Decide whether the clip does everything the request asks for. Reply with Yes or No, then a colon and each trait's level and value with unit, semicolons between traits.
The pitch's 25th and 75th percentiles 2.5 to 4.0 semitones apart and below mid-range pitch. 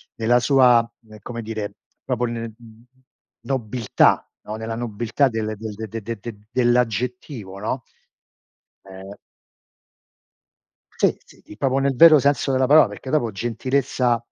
Yes: average, 2.9 semitones; low, 120 Hz